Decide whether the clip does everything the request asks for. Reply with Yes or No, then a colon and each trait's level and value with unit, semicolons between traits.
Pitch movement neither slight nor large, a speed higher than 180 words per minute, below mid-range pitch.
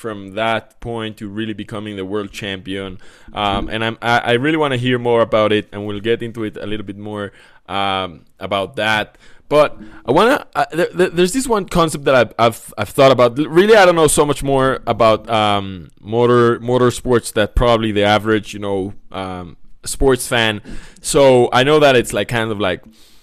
Yes: average, 3.4 semitones; average, 200 wpm; low, 110 Hz